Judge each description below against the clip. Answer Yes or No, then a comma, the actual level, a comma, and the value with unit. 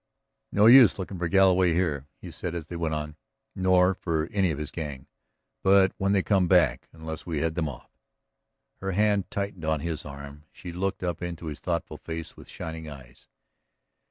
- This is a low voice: Yes, very low, 85 Hz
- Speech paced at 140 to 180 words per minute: No, average, 190 wpm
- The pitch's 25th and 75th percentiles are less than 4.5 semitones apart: Yes, average, 3.2 semitones